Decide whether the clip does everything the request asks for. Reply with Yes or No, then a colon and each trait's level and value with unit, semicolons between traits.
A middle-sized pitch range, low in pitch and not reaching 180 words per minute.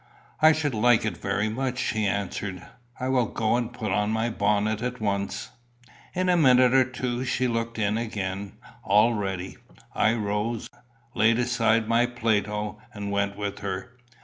Yes: average, 3.1 semitones; low, 110 Hz; average, 165 wpm